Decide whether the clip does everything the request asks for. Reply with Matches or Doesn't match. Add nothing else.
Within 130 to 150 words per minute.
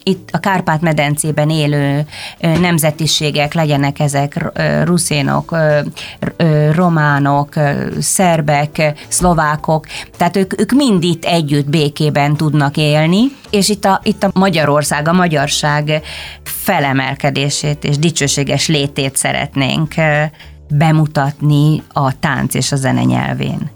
Doesn't match